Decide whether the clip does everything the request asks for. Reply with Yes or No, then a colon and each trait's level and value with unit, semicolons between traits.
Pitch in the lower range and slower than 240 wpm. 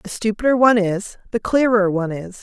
No: high, 210 Hz; average, 200 wpm